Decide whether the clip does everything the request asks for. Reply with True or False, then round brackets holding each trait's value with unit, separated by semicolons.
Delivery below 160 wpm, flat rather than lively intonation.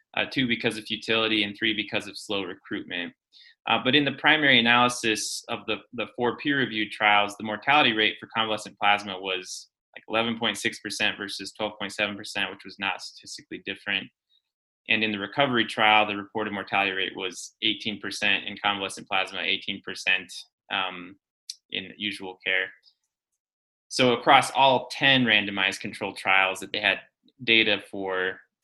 True (150 wpm; 2.3 semitones)